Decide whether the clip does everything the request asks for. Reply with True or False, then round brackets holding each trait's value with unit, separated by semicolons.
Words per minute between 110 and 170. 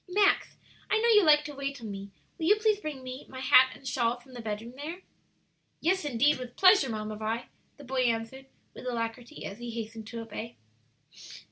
False (195 wpm)